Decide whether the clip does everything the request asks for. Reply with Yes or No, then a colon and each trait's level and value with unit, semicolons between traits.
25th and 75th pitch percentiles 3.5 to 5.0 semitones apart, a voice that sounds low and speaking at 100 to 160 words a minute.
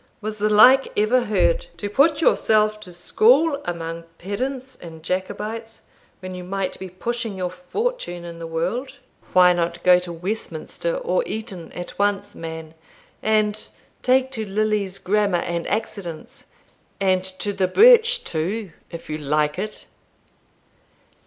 No: average, 4.4 semitones; high, 200 Hz; average, 140 wpm